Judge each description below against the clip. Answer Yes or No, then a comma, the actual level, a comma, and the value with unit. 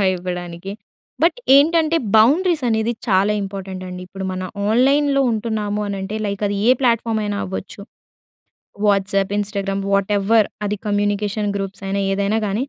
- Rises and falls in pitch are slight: Yes, narrow, 2.3 semitones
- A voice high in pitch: Yes, high, 205 Hz